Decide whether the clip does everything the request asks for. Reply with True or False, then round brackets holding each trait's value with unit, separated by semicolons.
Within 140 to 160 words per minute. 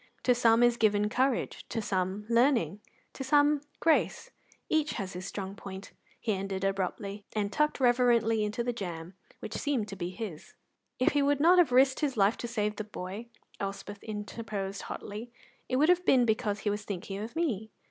False (185 wpm)